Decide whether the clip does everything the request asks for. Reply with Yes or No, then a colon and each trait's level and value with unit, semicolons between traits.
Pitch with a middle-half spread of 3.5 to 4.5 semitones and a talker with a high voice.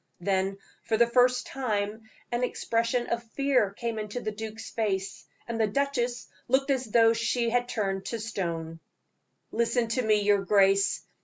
No: average, 3.0 semitones; high, 225 Hz